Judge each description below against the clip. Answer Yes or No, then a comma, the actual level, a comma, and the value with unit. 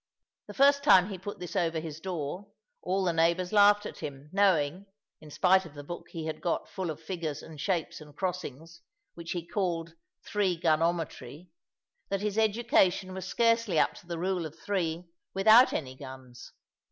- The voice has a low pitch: No, medium, 175 Hz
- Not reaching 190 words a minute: Yes, average, 180 wpm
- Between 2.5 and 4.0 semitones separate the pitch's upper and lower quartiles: Yes, average, 3.3 semitones